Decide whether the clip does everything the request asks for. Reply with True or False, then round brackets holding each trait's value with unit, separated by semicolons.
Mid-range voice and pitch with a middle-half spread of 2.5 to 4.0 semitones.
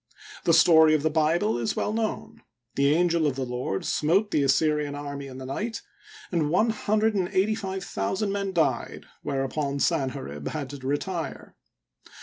False (155 Hz; 5.4 semitones)